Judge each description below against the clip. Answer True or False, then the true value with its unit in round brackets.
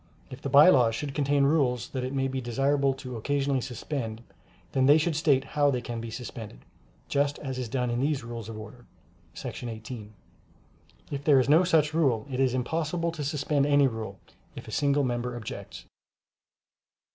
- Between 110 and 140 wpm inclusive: False (185 wpm)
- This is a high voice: False (135 Hz)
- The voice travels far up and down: False (3.1 semitones)